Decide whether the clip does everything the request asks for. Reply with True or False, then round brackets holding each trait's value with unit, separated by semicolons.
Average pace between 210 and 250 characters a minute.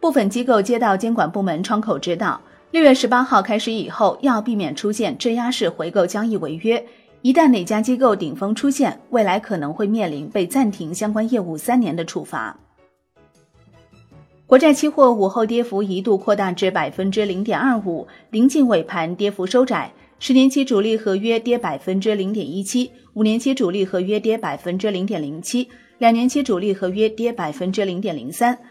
False (290 characters per minute)